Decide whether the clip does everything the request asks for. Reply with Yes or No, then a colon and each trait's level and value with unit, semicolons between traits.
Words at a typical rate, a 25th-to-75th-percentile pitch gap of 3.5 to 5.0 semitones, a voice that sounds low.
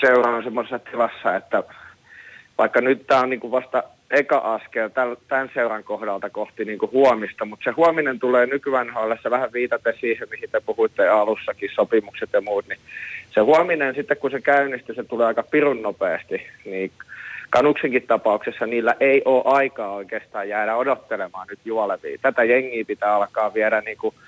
No: fast, 160 wpm; average, 4.1 semitones; low, 130 Hz